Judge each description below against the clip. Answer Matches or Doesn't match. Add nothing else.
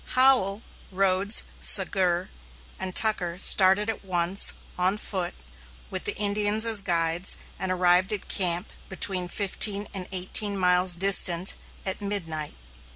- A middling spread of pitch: Doesn't match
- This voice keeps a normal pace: Doesn't match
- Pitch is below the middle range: Doesn't match